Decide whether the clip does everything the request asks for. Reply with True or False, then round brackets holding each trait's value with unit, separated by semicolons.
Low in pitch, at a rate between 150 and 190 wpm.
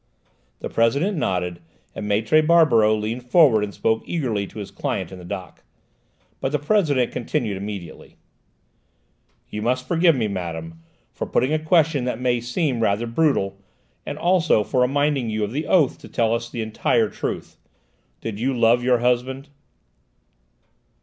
True (120 Hz; 155 wpm)